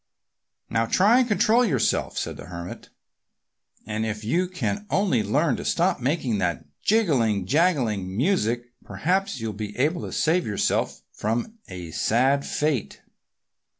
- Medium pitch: No, low, 125 Hz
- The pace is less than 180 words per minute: Yes, average, 140 wpm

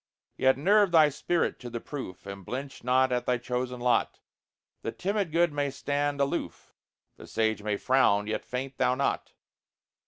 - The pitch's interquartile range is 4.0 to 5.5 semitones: No, average, 3.1 semitones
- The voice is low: Yes, low, 130 Hz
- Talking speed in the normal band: Yes, average, 165 wpm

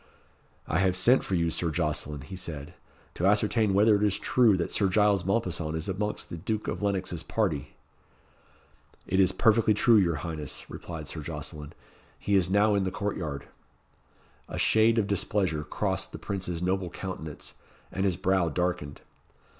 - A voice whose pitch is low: Yes, very low, 95 Hz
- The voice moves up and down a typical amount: Yes, average, 3.6 semitones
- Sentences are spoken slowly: No, average, 170 wpm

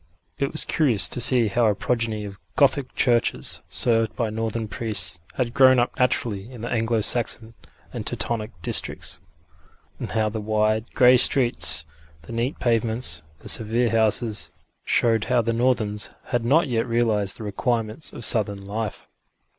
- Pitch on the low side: Yes, low, 115 Hz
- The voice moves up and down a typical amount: No, narrow, 2.2 semitones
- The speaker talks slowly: No, average, 155 wpm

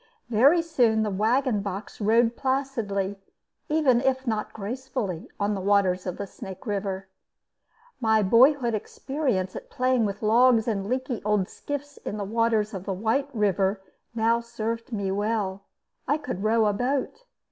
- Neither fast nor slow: Yes, average, 150 wpm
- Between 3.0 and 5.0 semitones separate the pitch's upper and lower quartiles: Yes, average, 4.1 semitones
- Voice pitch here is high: Yes, high, 220 Hz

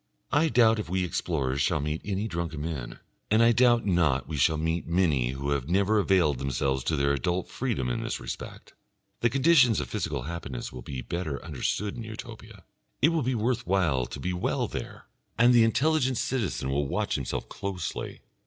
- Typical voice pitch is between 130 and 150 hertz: No, very low, 90 Hz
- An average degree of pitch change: No, wide, 8.0 semitones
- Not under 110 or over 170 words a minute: No, average, 190 wpm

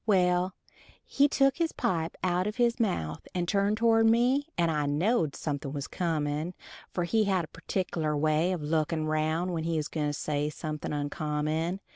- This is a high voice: No, medium, 170 Hz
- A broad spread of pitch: No, average, 4.5 semitones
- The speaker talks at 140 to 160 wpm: No, average, 180 wpm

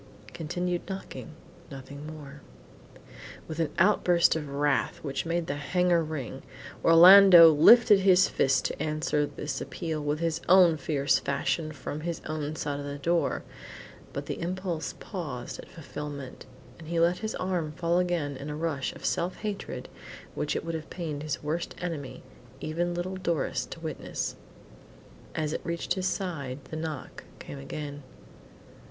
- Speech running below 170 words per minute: Yes, average, 155 wpm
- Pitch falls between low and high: Yes, medium, 160 Hz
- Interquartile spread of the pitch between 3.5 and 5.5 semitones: No, average, 3.1 semitones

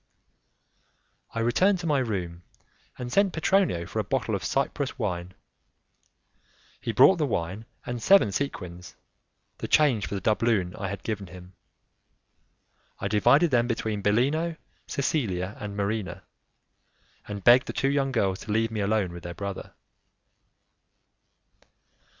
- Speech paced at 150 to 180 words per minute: No, average, 140 wpm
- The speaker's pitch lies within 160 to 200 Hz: No, low, 110 Hz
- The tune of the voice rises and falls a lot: Yes, wide, 5.9 semitones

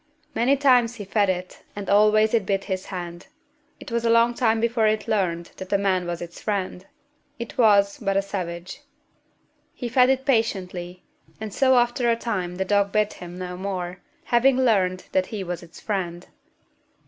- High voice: Yes, high, 200 Hz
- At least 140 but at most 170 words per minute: No, average, 185 wpm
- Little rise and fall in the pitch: No, average, 4.1 semitones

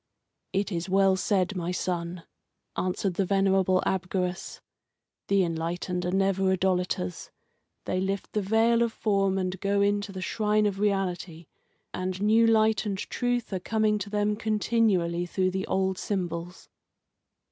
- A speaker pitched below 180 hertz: No, high, 190 Hz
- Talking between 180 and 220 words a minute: No, average, 145 wpm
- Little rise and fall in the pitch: Yes, narrow, 2.2 semitones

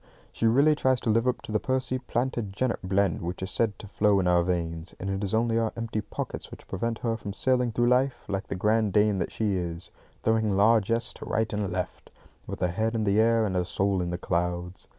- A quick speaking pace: Yes, fast, 230 wpm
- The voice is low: Yes, low, 105 Hz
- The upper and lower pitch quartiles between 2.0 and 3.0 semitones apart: No, average, 3.6 semitones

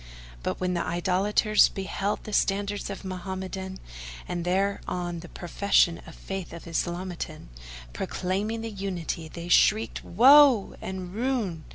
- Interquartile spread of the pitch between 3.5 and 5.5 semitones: No, narrow, 2.5 semitones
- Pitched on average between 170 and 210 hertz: Yes, high, 190 Hz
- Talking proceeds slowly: Yes, slow, 125 wpm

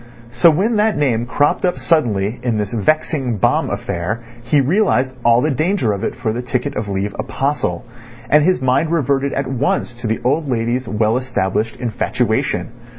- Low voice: Yes, low, 125 Hz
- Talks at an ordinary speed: Yes, average, 175 wpm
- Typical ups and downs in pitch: Yes, average, 4.5 semitones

